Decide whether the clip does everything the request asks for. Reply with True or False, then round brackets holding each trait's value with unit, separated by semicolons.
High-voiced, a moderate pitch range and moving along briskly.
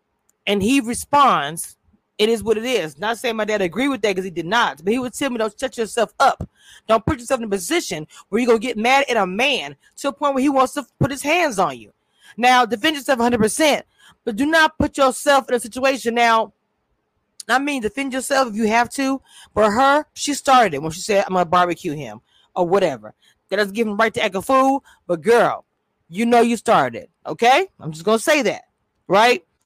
True (235 Hz; 4.4 semitones; 225 wpm)